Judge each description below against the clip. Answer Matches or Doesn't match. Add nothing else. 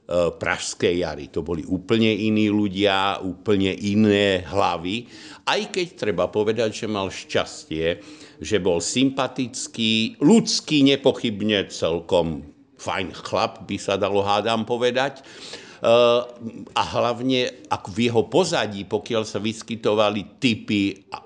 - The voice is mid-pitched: Doesn't match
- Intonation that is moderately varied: Matches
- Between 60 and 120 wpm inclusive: Matches